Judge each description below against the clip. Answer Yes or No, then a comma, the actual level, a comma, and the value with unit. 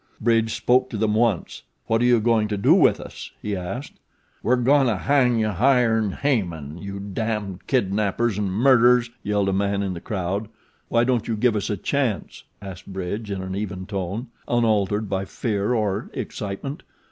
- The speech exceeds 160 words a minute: Yes, average, 180 wpm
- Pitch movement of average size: Yes, average, 3.3 semitones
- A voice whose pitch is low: Yes, low, 105 Hz